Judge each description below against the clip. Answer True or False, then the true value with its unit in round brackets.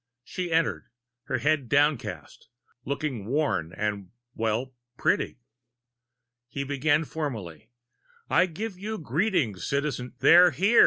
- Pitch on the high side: False (145 Hz)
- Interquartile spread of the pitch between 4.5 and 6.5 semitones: True (5.5 semitones)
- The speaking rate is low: True (115 wpm)